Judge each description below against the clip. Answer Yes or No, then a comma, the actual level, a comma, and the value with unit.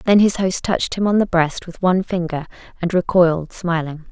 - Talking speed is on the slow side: No, fast, 205 wpm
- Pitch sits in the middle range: Yes, medium, 180 Hz